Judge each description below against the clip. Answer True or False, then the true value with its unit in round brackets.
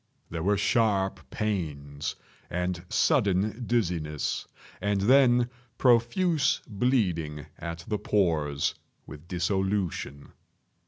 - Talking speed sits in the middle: False (90 wpm)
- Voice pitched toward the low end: True (95 Hz)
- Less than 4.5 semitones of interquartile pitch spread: False (5.5 semitones)